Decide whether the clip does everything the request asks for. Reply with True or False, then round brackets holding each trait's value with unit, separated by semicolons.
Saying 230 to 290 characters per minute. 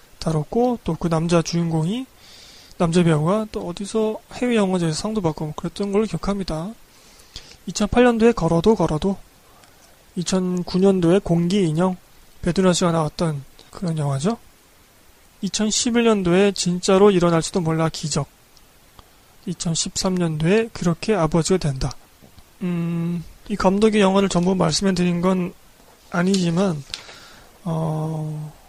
True (245 characters per minute)